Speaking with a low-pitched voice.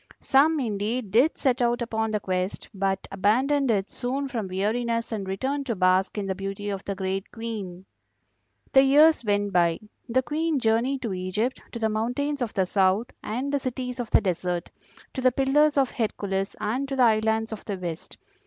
No: high, 225 Hz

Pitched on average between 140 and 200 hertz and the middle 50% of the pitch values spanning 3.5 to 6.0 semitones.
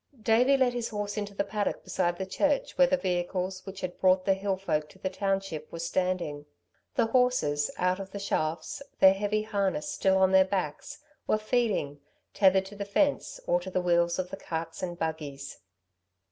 No: high, 190 Hz; average, 2.7 semitones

